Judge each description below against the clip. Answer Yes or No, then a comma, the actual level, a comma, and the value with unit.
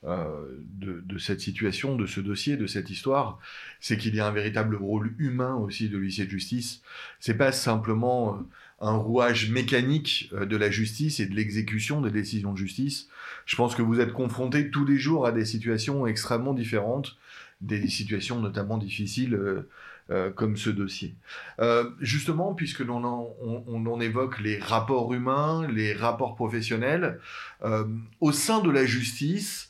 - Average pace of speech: Yes, average, 170 wpm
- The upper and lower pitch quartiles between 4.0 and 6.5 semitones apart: No, average, 3.5 semitones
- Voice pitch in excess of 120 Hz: No, low, 115 Hz